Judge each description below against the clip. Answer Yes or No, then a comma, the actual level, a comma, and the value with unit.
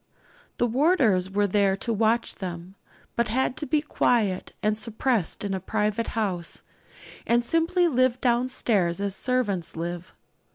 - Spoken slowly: No, average, 150 wpm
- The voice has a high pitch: Yes, high, 220 Hz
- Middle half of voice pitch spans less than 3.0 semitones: No, average, 4.6 semitones